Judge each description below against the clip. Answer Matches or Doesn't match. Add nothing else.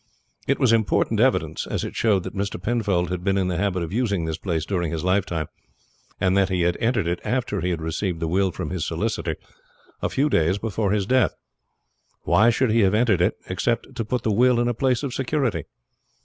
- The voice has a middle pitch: Doesn't match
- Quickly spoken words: Matches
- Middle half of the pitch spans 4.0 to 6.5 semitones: Matches